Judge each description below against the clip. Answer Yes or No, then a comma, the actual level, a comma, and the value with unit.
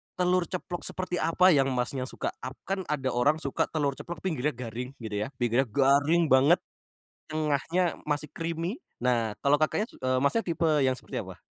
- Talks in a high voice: No, medium, 145 Hz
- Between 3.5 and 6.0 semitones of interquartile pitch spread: Yes, average, 4.7 semitones